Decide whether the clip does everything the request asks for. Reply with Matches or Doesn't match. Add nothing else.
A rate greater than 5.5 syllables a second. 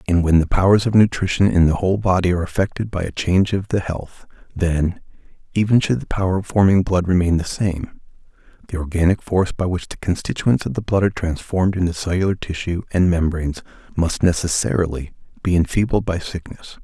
Matches